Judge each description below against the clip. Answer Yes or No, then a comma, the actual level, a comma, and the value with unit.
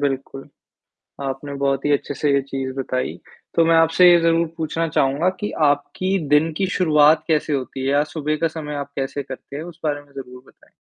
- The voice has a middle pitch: Yes, medium, 145 Hz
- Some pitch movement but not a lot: Yes, average, 3.0 semitones